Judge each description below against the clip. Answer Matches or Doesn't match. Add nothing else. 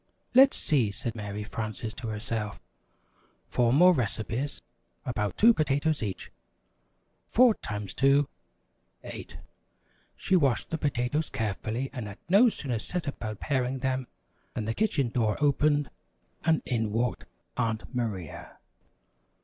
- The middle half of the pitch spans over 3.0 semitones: Matches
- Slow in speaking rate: Matches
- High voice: Doesn't match